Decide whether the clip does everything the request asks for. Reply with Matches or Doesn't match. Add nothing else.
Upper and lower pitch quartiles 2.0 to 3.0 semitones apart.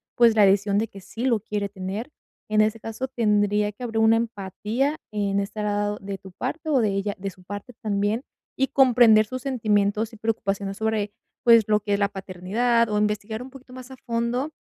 Matches